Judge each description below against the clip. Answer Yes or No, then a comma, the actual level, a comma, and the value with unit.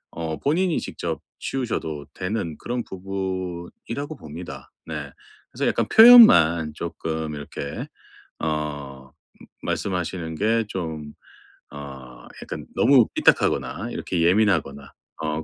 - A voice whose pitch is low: Yes, very low, 85 Hz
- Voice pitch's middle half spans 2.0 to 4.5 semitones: No, wide, 5.6 semitones